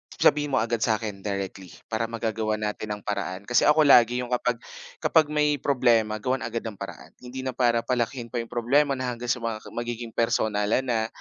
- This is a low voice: Yes, low, 115 Hz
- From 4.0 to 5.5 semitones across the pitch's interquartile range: No, narrow, 2.6 semitones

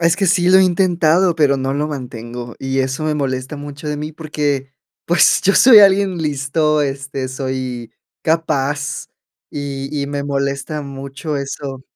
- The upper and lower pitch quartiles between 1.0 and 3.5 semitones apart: Yes, average, 2.8 semitones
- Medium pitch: Yes, medium, 145 Hz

